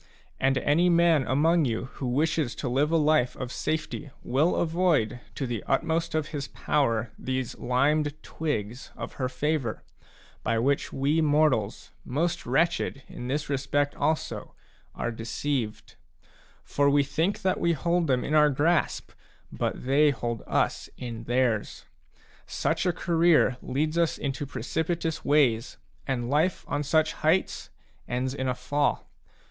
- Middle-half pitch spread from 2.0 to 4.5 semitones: Yes, average, 3.8 semitones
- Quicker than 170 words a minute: No, average, 145 wpm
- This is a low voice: No, medium, 145 Hz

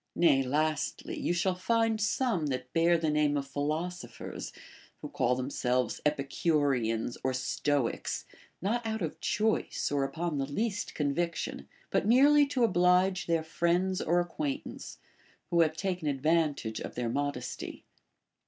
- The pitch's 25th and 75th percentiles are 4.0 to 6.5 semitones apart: Yes, average, 4.6 semitones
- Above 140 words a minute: No, slow, 135 wpm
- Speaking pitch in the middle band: Yes, medium, 160 Hz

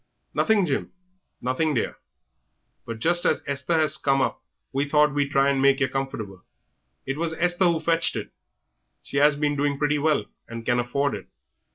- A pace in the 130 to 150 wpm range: No, average, 180 wpm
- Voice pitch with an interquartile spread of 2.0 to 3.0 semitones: Yes, narrow, 2.6 semitones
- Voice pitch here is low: No, medium, 145 Hz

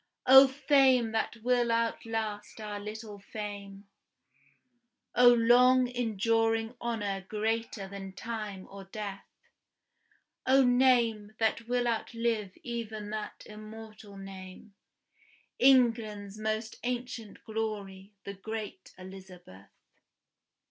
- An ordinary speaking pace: No, slow, 95 wpm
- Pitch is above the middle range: Yes, high, 220 Hz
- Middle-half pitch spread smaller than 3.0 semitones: Yes, narrow, 2.6 semitones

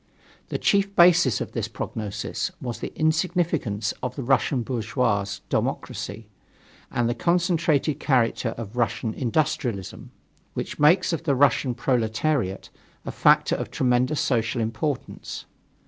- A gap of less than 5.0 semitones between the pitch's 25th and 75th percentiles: No, average, 5.3 semitones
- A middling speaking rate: No, slow, 125 wpm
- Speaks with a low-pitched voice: Yes, low, 125 Hz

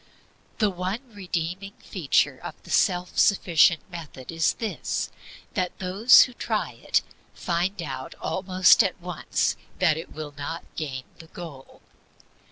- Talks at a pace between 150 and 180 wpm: No, slow, 135 wpm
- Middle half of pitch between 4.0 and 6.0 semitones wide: No, average, 3.2 semitones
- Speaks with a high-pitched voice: No, medium, 175 Hz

